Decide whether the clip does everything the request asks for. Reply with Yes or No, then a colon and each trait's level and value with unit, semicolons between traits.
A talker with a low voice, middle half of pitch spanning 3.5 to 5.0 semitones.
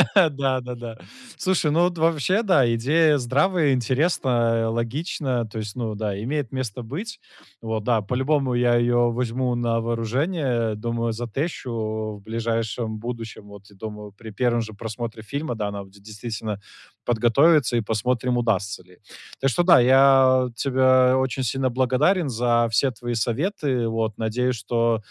No: low, 120 Hz; average, 3.0 semitones